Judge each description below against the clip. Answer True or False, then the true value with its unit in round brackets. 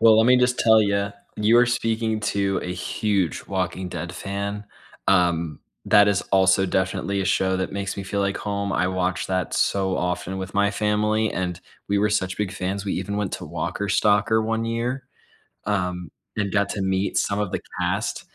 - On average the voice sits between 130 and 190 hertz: False (100 Hz)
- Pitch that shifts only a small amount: True (2.2 semitones)